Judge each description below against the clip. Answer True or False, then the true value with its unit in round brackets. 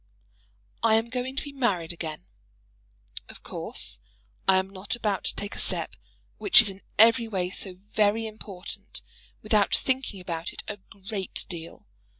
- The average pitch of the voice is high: True (205 Hz)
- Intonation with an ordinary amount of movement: True (3.3 semitones)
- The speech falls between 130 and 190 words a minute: True (155 wpm)